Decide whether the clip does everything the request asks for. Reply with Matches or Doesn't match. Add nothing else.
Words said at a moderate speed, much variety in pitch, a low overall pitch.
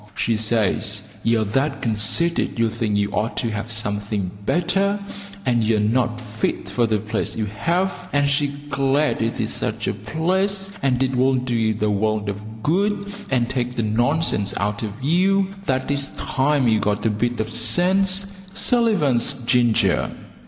Matches